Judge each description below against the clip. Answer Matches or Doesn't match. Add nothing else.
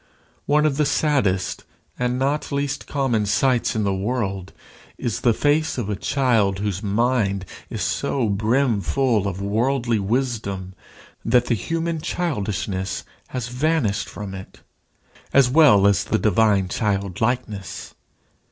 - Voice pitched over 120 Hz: Doesn't match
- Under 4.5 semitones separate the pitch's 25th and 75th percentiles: Doesn't match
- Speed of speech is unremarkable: Doesn't match